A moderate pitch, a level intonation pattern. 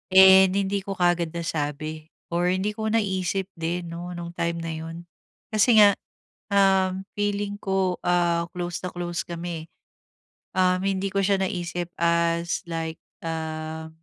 Yes: medium, 175 Hz; narrow, 2.2 semitones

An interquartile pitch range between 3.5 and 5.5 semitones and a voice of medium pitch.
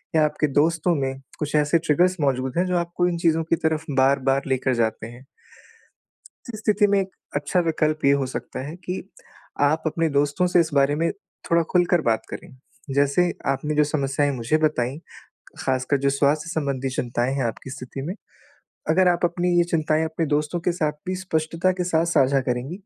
Yes: average, 3.8 semitones; medium, 155 Hz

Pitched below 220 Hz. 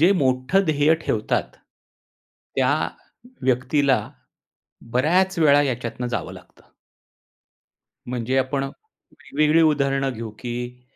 Yes: low, 135 Hz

